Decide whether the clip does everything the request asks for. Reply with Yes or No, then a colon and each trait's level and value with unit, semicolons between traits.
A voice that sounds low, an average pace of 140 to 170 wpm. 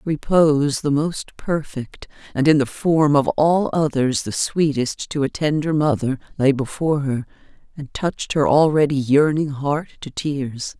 No: medium, 145 Hz; average, 155 wpm